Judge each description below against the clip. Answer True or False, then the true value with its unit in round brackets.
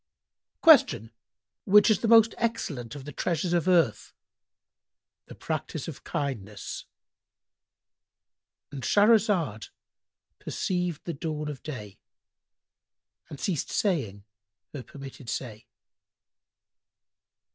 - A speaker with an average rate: False (90 wpm)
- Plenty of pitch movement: True (7.2 semitones)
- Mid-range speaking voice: True (150 Hz)